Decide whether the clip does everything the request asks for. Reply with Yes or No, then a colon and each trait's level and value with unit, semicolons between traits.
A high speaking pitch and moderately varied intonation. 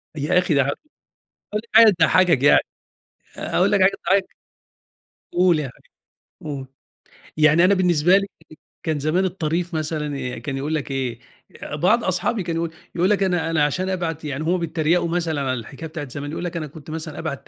No: medium, 165 Hz; average, 3.5 semitones